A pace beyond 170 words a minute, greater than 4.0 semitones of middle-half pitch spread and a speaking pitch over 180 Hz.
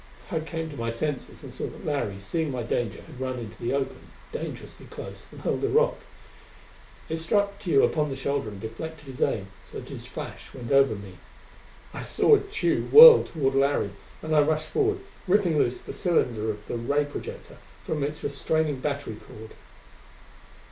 No: average, 180 wpm; wide, 5.4 semitones; medium, 140 Hz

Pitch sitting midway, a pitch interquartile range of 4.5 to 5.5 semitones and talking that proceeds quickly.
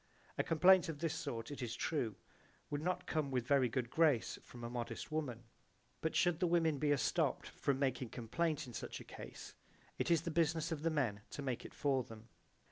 Yes: medium, 145 Hz; average, 4.8 semitones; fast, 210 wpm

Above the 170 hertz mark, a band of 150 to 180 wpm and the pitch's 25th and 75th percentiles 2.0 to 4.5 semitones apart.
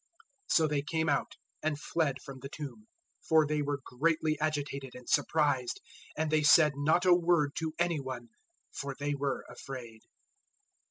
No: medium, 145 Hz; average, 165 wpm; narrow, 2.4 semitones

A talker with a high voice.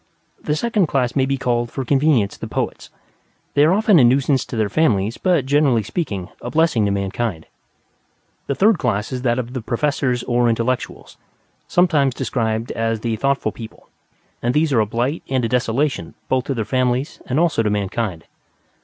No: low, 125 Hz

